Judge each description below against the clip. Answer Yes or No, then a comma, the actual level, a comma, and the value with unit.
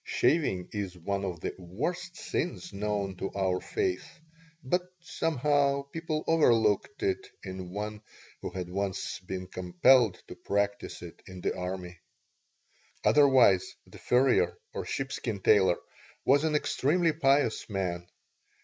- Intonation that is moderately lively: No, wide, 8.0 semitones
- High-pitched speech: No, low, 105 Hz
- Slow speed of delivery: Yes, slow, 130 wpm